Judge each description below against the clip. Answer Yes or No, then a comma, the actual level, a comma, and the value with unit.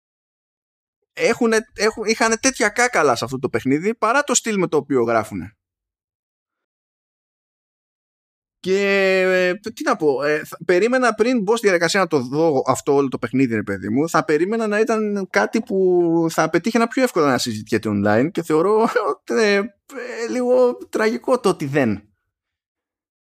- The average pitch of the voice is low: No, medium, 185 Hz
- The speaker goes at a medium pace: Yes, average, 155 wpm